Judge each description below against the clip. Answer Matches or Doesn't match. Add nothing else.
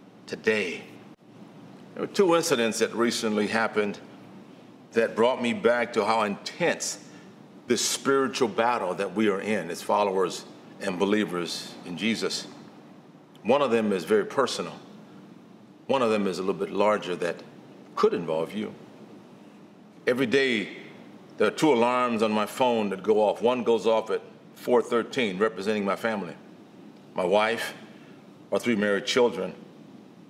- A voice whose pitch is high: Doesn't match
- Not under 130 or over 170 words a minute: Matches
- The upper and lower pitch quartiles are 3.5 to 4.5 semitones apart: Doesn't match